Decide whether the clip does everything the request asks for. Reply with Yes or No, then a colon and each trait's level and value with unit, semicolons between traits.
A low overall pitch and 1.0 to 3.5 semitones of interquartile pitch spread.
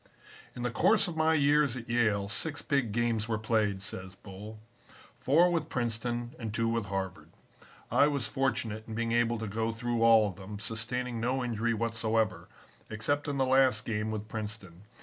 Yes: low, 115 Hz; narrow, 2.6 semitones